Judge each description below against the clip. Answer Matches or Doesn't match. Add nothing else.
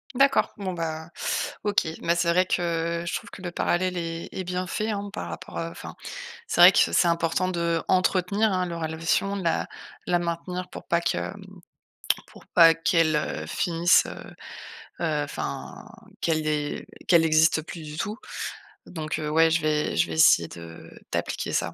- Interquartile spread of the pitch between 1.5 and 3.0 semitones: Matches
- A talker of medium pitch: Matches